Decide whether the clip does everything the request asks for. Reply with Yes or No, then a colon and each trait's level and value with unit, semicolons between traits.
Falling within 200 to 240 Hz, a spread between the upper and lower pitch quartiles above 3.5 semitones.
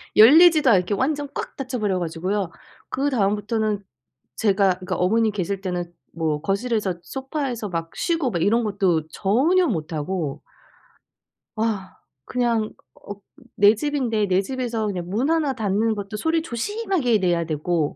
Yes: high, 210 Hz; wide, 5.5 semitones